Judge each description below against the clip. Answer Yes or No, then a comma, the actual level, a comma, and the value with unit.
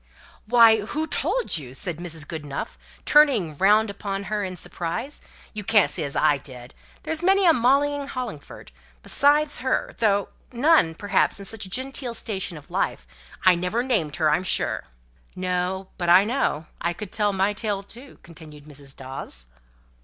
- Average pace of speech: Yes, average, 170 wpm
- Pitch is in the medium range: No, high, 195 Hz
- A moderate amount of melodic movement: No, wide, 6.8 semitones